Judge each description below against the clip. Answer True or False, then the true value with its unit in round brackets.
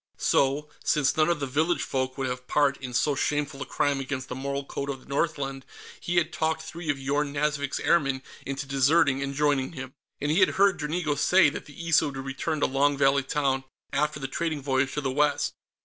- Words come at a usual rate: False (215 wpm)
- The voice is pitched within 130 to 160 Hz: True (140 Hz)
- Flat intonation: True (1.9 semitones)